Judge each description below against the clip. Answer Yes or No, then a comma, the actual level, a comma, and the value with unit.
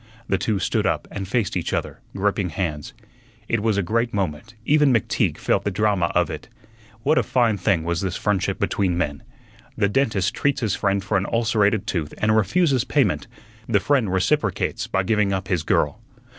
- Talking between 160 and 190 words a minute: Yes, average, 185 wpm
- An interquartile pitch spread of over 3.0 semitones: Yes, average, 3.6 semitones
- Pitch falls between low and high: No, low, 100 Hz